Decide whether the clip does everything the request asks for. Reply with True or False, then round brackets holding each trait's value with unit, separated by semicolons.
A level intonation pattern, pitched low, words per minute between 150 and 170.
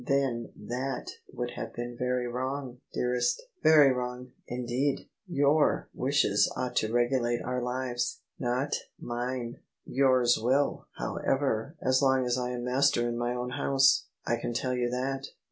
True (1.7 semitones; 125 Hz; 160 wpm)